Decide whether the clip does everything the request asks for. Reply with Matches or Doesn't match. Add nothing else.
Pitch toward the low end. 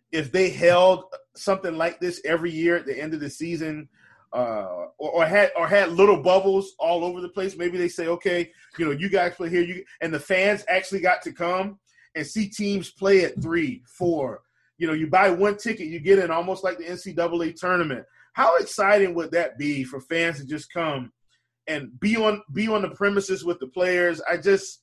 Doesn't match